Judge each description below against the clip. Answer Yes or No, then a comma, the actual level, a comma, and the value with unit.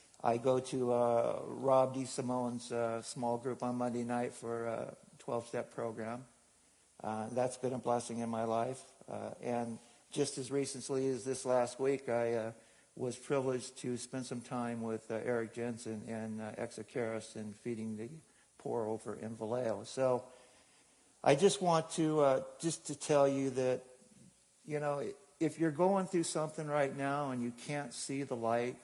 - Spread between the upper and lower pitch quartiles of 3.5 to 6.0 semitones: No, average, 2.9 semitones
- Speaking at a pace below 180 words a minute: Yes, average, 170 wpm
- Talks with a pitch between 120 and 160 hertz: Yes, low, 125 Hz